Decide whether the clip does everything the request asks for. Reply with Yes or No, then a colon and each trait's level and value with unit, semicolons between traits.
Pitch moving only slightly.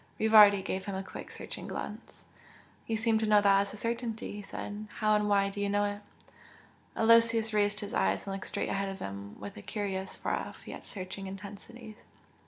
Yes: narrow, 1.8 semitones